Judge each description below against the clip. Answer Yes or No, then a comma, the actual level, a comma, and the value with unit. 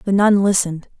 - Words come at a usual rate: Yes, average, 180 wpm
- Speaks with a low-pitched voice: No, high, 195 Hz